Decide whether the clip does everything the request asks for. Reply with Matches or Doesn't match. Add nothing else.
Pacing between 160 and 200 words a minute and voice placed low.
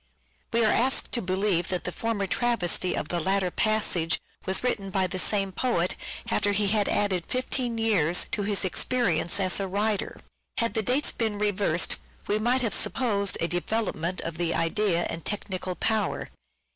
Doesn't match